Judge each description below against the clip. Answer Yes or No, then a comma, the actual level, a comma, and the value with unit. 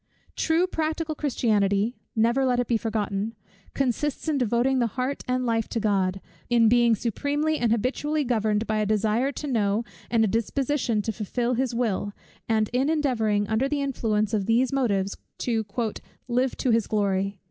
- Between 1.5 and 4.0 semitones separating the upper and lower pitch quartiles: Yes, average, 3.6 semitones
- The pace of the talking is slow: No, average, 170 wpm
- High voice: Yes, high, 235 Hz